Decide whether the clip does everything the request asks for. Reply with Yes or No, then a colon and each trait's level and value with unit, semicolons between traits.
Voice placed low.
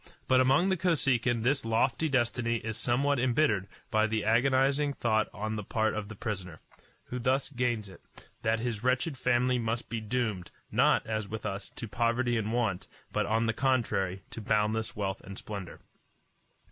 Yes: low, 115 Hz